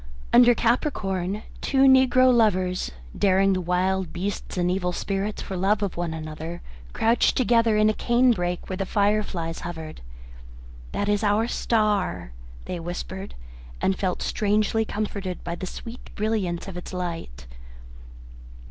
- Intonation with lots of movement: No, average, 3.4 semitones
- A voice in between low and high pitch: No, high, 195 Hz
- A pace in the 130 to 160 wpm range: Yes, average, 145 wpm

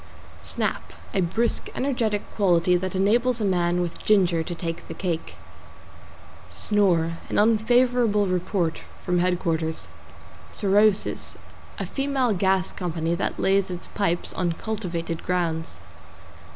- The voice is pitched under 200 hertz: Yes, medium, 185 Hz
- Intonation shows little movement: No, average, 3.5 semitones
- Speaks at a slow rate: Yes, slow, 120 wpm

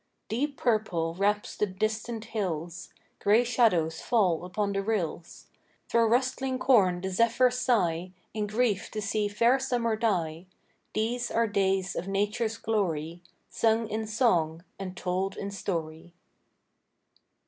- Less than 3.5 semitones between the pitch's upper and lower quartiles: No, average, 4.1 semitones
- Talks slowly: Yes, slow, 130 wpm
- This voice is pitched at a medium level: No, high, 210 Hz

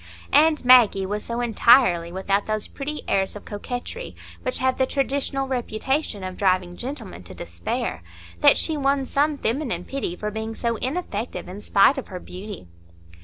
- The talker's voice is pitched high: Yes, high, 230 Hz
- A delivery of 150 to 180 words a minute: Yes, average, 165 wpm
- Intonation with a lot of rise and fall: Yes, wide, 5.7 semitones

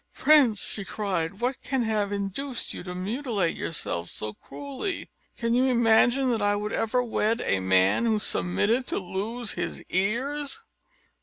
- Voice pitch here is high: Yes, high, 220 Hz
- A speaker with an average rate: Yes, average, 155 wpm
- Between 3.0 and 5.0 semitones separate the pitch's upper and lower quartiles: Yes, average, 4.7 semitones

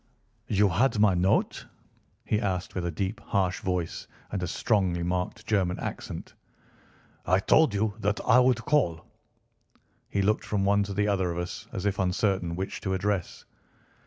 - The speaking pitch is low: Yes, very low, 95 Hz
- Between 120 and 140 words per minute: No, average, 165 wpm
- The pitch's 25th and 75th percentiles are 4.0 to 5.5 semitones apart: No, narrow, 2.5 semitones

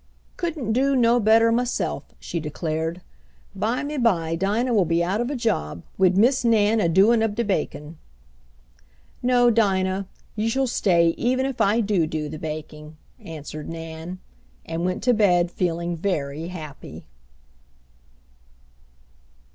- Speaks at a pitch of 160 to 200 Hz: Yes, high, 190 Hz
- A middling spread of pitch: No, wide, 6.0 semitones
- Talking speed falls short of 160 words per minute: Yes, average, 140 wpm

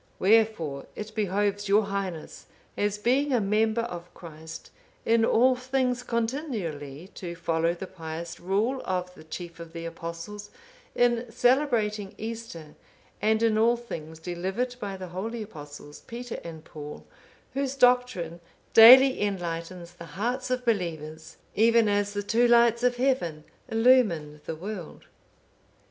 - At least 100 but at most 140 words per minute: Yes, slow, 135 wpm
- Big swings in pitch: Yes, wide, 5.8 semitones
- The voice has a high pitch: Yes, high, 205 Hz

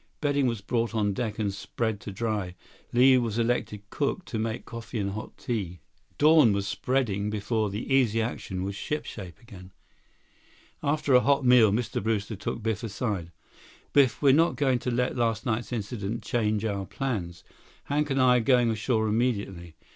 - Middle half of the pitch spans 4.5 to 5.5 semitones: No, average, 3.5 semitones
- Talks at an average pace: Yes, average, 170 wpm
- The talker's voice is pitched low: Yes, low, 115 Hz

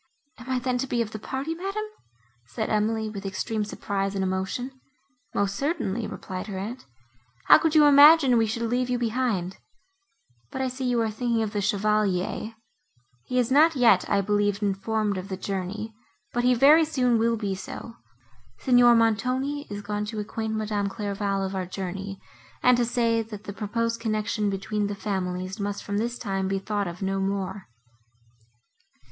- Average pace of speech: Yes, average, 175 wpm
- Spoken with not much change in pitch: No, average, 3.5 semitones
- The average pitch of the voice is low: No, high, 215 Hz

